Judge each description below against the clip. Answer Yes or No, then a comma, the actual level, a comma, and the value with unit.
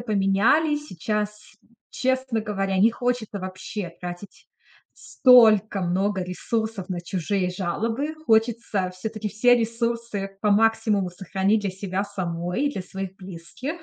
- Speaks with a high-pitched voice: Yes, high, 205 Hz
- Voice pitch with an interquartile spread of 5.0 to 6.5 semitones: No, average, 3.3 semitones